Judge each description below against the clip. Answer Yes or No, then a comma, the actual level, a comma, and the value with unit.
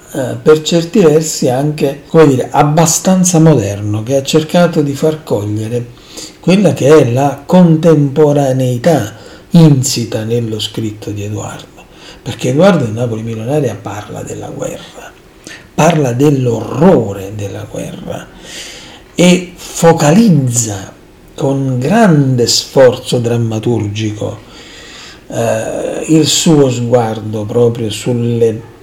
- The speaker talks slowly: Yes, slow, 100 wpm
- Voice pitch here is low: Yes, low, 130 Hz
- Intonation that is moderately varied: No, wide, 5.7 semitones